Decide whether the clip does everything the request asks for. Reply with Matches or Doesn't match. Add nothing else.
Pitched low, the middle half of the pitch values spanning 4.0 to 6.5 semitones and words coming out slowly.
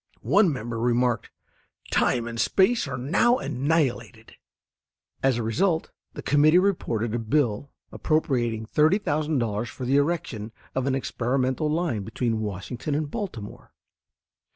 Matches